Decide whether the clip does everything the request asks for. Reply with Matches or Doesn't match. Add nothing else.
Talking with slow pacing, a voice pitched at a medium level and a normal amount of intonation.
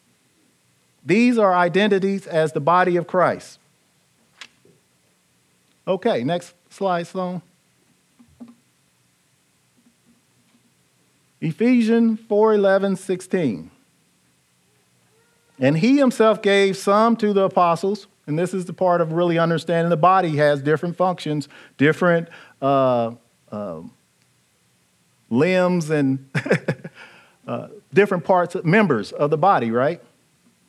Doesn't match